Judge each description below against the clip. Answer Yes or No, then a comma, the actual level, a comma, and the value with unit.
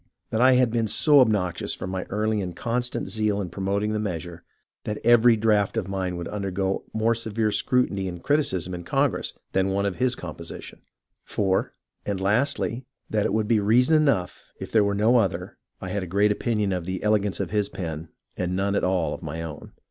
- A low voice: Yes, low, 100 Hz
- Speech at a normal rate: No, fast, 210 wpm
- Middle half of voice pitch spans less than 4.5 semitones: Yes, average, 3.2 semitones